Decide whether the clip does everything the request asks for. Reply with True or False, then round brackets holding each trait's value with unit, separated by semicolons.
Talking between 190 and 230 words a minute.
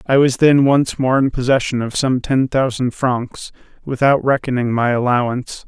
False (170 wpm)